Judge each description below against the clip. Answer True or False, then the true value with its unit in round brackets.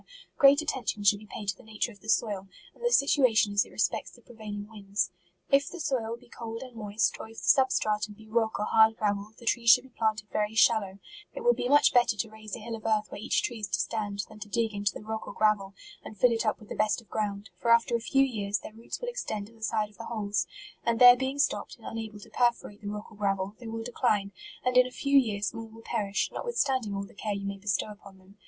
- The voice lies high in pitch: True (220 Hz)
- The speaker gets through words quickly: True (270 wpm)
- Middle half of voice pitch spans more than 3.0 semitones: False (2.5 semitones)